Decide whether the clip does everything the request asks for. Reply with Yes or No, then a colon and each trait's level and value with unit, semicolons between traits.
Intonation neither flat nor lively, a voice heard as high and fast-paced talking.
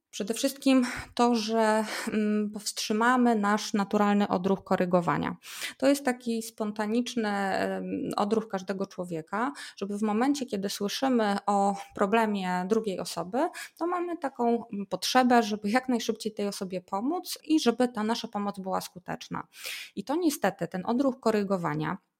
No: average, 3.6 semitones; high, 215 Hz; average, 130 wpm